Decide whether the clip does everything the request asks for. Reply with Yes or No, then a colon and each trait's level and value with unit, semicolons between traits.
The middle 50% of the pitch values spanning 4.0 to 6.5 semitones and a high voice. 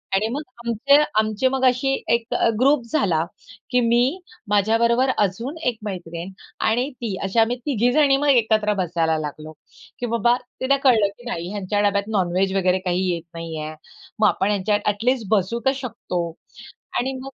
Yes: average, 4.9 semitones; high, 220 Hz